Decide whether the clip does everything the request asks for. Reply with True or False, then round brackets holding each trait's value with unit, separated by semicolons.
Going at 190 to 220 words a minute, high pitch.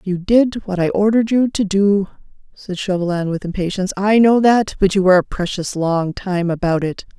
True (200 wpm; 195 Hz)